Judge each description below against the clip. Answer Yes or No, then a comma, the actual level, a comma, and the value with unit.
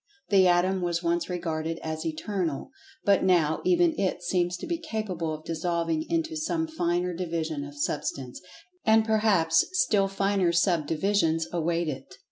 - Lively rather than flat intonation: No, average, 3.7 semitones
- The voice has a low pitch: No, medium, 175 Hz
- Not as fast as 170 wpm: Yes, average, 140 wpm